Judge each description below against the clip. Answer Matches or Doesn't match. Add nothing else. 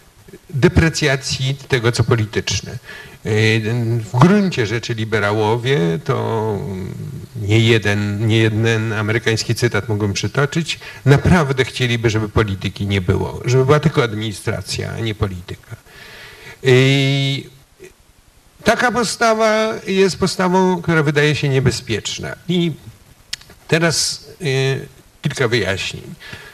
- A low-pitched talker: Matches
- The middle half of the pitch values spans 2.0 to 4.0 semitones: Doesn't match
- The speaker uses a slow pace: Matches